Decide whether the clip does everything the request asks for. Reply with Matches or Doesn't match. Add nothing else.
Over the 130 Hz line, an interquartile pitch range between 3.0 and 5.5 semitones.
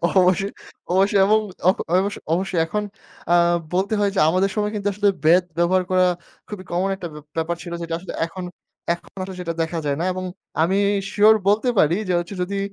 Doesn't match